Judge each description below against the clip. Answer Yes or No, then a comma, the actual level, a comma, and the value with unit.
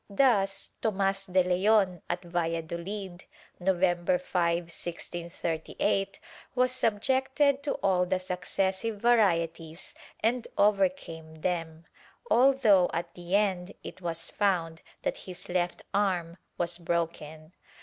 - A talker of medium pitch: Yes, medium, 180 Hz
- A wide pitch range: No, average, 2.9 semitones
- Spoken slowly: Yes, slow, 110 wpm